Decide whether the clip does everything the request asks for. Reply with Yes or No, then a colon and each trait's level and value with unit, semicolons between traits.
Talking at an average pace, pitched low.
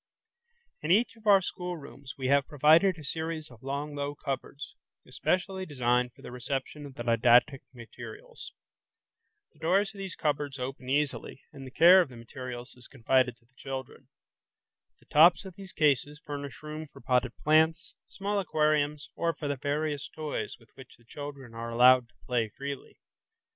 No: average, 170 wpm; medium, 145 Hz